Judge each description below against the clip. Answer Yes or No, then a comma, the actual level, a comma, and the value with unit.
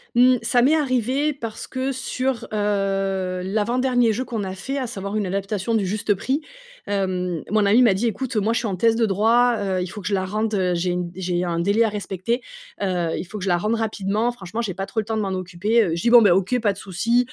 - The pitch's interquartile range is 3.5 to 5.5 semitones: Yes, average, 3.8 semitones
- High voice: Yes, high, 210 Hz